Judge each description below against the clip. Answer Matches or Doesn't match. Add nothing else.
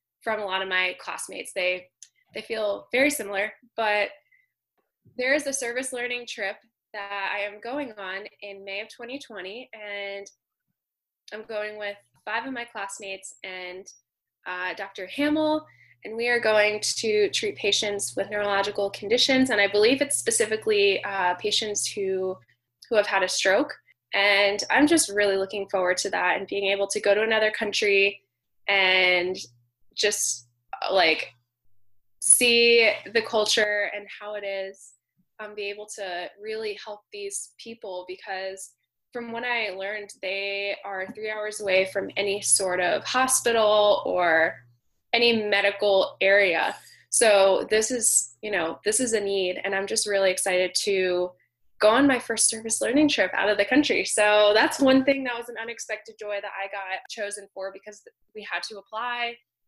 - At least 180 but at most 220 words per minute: Doesn't match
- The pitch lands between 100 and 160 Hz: Doesn't match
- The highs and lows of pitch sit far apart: Doesn't match